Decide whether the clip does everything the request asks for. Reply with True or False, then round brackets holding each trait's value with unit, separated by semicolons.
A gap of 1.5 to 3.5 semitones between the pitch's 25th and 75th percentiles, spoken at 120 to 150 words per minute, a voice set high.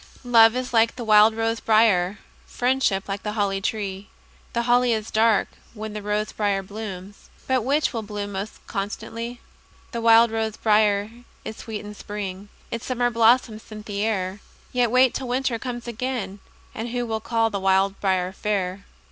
False (2.6 semitones; 175 wpm; 220 Hz)